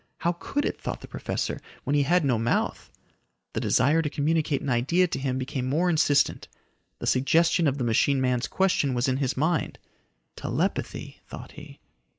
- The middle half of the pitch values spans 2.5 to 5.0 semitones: Yes, average, 4.1 semitones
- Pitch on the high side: No, medium, 140 Hz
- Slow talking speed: No, average, 175 wpm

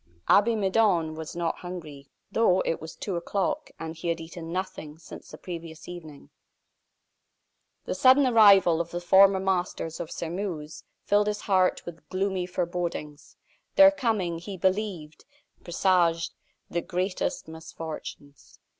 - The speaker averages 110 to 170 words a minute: Yes, slow, 135 wpm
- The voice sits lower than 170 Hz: No, medium, 175 Hz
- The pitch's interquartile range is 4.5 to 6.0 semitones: No, average, 3.0 semitones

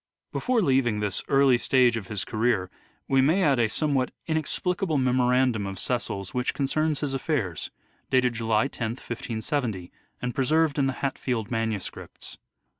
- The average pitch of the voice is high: No, low, 125 Hz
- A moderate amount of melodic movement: Yes, average, 3.9 semitones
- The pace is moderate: Yes, average, 160 wpm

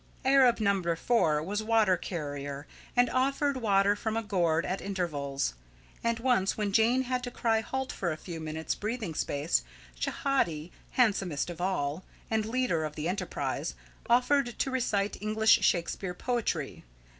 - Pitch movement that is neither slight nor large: No, wide, 6.2 semitones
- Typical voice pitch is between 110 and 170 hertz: No, high, 205 Hz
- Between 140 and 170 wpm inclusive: Yes, average, 150 wpm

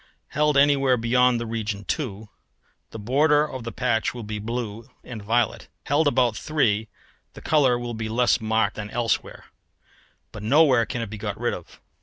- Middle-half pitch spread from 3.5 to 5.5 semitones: No, average, 3.1 semitones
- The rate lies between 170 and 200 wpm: Yes, average, 175 wpm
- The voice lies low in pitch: Yes, low, 120 Hz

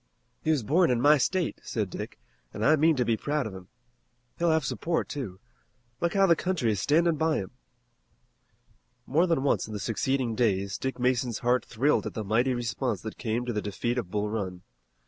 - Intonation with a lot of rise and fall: Yes, wide, 5.8 semitones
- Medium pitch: No, low, 125 Hz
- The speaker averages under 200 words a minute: No, fast, 205 wpm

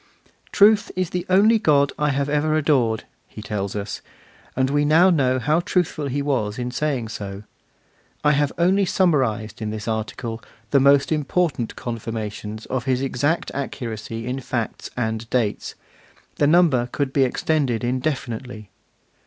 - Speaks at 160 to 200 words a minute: No, average, 150 wpm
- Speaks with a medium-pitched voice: No, low, 130 Hz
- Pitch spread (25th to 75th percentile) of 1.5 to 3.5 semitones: No, average, 4.9 semitones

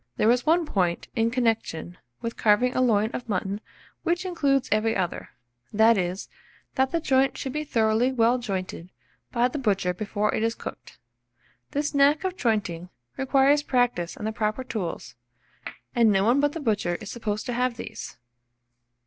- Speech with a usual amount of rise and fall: Yes, average, 4.4 semitones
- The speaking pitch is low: No, high, 230 Hz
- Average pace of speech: Yes, average, 170 wpm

